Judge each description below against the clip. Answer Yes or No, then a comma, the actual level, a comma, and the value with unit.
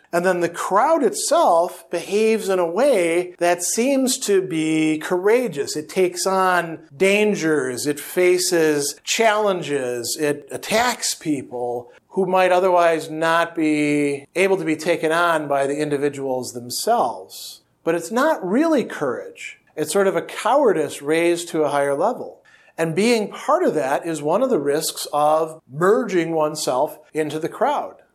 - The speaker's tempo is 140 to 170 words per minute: Yes, average, 145 wpm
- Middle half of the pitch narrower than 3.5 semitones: No, average, 4.3 semitones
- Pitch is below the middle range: No, medium, 170 Hz